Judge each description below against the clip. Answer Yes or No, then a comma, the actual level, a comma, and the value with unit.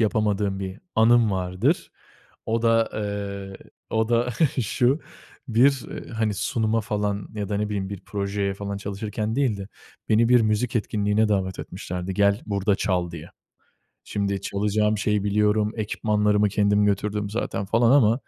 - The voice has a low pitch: Yes, low, 105 Hz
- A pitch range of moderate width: No, narrow, 1.9 semitones